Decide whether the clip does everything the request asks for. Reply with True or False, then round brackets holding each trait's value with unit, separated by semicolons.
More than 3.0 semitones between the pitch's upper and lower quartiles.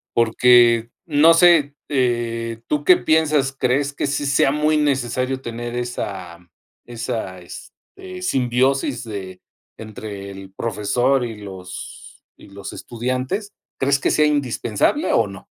True (3.8 semitones)